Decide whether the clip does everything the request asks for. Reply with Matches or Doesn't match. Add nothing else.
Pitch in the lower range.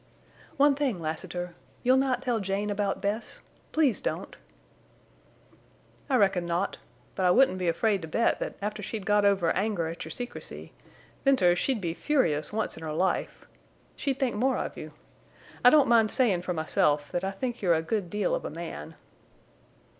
Doesn't match